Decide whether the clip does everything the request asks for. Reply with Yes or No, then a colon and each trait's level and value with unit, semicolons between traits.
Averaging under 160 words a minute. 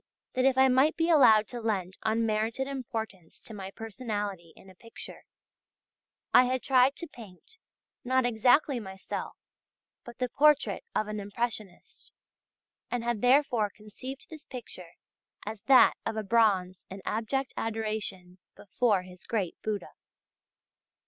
Yes: slow, 135 wpm